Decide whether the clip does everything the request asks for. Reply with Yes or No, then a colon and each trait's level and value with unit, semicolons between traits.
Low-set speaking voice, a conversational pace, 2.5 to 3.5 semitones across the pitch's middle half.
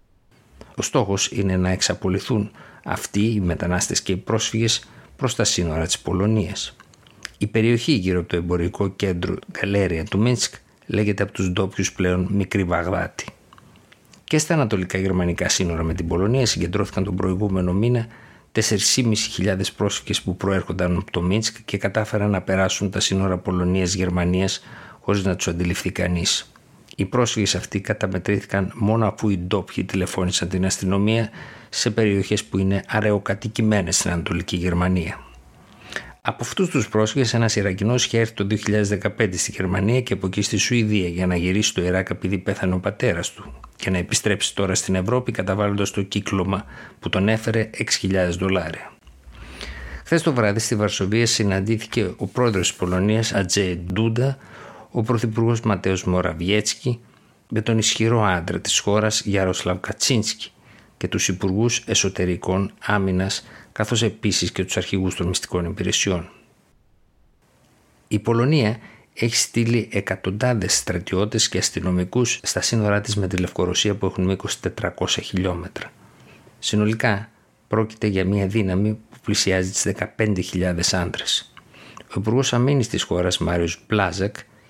Yes: low, 100 Hz; average, 140 wpm; average, 3.0 semitones